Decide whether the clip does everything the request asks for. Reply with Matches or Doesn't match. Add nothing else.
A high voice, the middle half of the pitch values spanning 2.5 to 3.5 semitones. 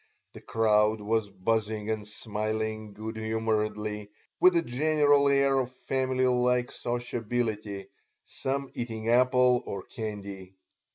Doesn't match